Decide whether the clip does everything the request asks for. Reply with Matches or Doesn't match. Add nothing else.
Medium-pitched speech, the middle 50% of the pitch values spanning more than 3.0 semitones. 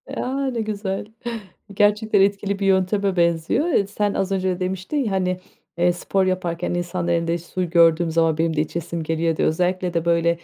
Doesn't match